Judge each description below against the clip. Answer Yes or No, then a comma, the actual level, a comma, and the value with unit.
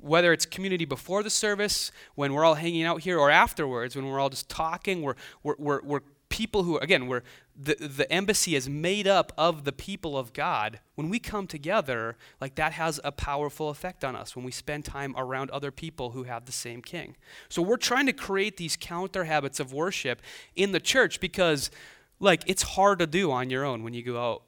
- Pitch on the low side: No, medium, 155 Hz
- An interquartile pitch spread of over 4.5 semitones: Yes, average, 5.2 semitones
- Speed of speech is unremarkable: No, fast, 220 wpm